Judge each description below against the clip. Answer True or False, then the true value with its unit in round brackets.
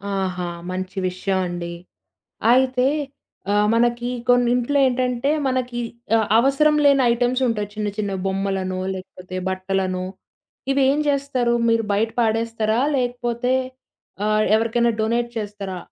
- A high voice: True (230 Hz)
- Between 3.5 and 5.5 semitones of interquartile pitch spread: True (4.3 semitones)